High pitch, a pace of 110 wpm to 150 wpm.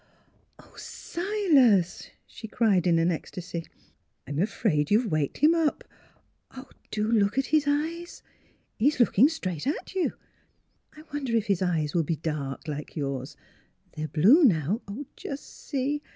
Yes: high, 210 Hz; average, 145 wpm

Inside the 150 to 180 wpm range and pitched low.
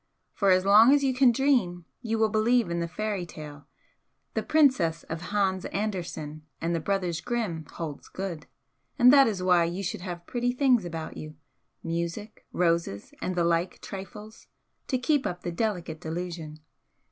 No: average, 170 wpm; medium, 185 Hz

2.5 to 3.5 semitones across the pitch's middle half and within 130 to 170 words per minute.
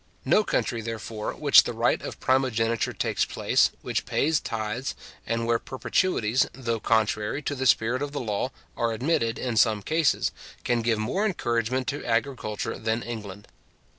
Yes: average, 3.0 semitones; average, 160 wpm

